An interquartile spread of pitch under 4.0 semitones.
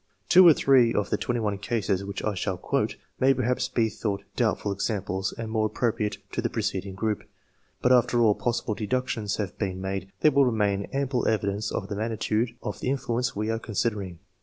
Yes: average, 3.3 semitones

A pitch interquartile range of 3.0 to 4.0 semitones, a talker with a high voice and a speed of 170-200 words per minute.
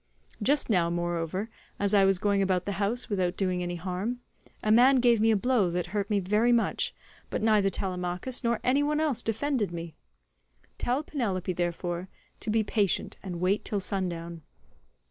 No: average, 4.4 semitones; high, 200 Hz; average, 175 wpm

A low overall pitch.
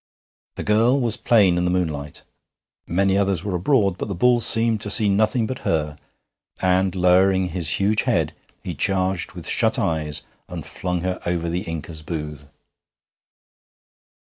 Yes: very low, 95 Hz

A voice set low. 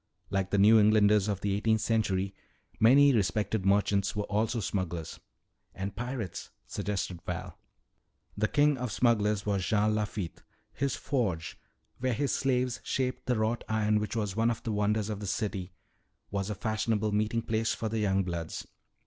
Yes: low, 105 Hz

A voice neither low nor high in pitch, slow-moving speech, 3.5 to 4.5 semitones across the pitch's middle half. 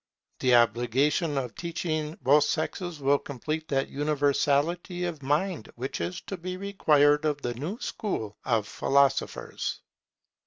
Yes: medium, 145 Hz; slow, 130 wpm; average, 3.8 semitones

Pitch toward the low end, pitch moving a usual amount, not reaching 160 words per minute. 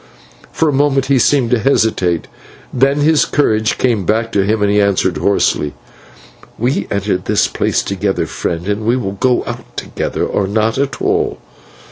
No: low, 110 Hz; average, 4.6 semitones; average, 170 wpm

